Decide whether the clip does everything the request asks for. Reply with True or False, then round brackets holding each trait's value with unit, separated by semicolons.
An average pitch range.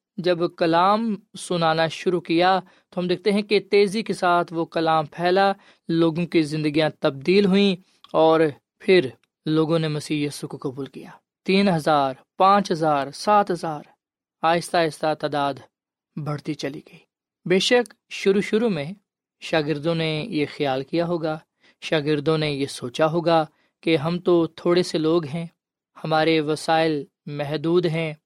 True (3.2 semitones)